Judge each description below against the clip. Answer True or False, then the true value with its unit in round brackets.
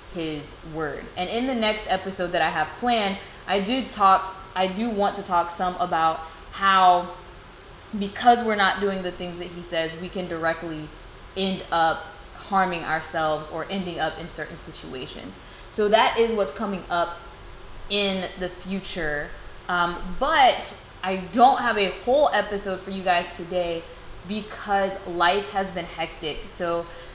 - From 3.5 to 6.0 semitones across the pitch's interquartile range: False (2.8 semitones)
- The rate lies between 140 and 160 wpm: True (155 wpm)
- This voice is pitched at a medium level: True (180 Hz)